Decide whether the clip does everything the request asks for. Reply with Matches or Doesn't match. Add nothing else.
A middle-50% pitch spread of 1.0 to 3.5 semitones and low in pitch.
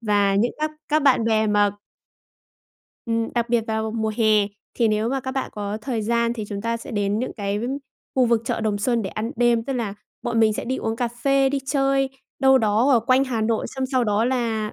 Doesn't match